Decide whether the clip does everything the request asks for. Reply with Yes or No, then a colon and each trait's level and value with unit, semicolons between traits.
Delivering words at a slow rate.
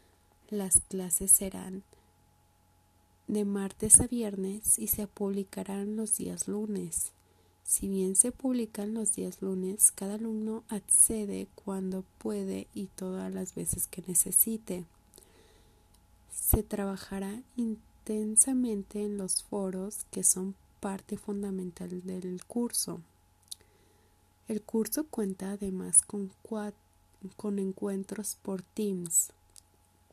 Yes: slow, 105 wpm